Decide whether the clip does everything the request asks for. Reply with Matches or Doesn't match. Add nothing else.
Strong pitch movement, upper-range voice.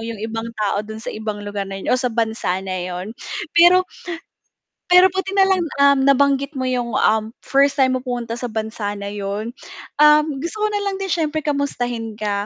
Matches